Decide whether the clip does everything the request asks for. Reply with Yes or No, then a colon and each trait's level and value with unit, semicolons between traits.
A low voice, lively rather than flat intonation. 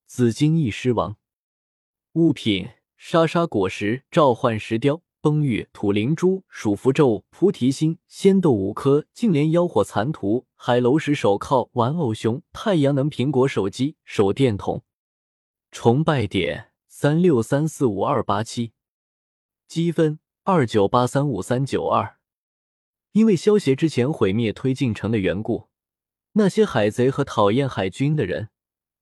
Yes: low, 130 Hz; wide, 6.2 semitones